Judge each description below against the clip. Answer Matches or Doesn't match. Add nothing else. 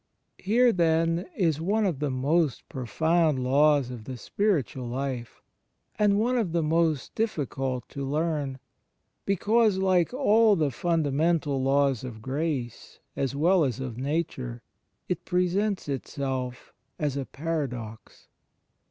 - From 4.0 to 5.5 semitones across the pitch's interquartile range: Matches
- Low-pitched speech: Doesn't match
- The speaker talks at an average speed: Doesn't match